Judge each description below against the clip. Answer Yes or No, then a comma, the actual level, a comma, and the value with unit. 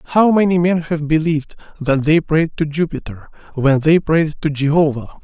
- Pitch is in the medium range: Yes, medium, 155 Hz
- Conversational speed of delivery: Yes, average, 170 wpm